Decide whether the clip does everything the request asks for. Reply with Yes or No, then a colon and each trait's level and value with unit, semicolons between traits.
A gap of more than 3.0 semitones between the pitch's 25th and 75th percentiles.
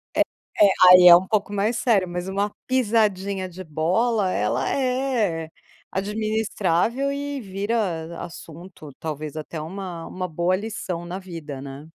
Yes: average, 4.3 semitones